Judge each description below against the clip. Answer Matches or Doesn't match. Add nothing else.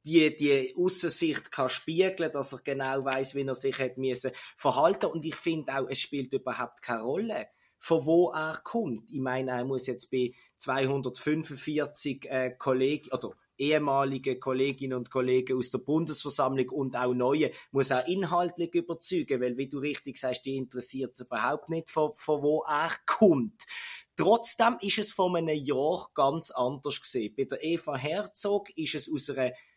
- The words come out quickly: Doesn't match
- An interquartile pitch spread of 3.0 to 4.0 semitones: Matches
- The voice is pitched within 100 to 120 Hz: Doesn't match